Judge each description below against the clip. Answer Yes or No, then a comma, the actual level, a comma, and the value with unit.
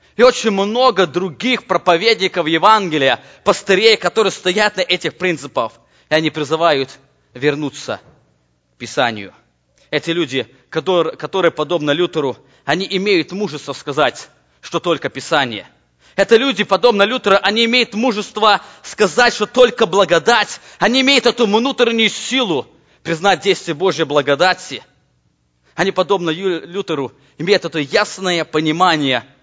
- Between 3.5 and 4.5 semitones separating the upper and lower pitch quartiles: No, wide, 5.6 semitones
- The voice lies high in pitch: No, medium, 180 Hz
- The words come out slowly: Yes, slow, 115 wpm